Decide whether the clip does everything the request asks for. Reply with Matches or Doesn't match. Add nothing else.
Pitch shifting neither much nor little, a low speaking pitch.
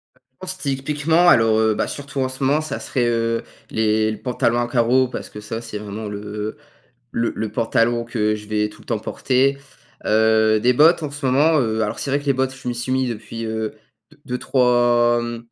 Matches